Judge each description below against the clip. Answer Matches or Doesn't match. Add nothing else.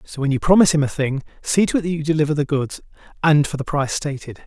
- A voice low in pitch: Doesn't match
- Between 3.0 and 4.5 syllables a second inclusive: Doesn't match